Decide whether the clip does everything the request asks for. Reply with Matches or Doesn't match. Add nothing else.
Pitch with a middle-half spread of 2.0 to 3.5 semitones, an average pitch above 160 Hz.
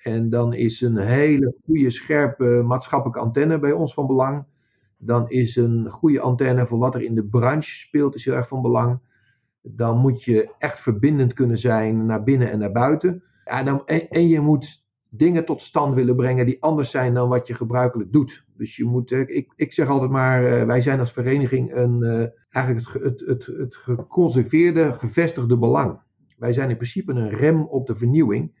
Doesn't match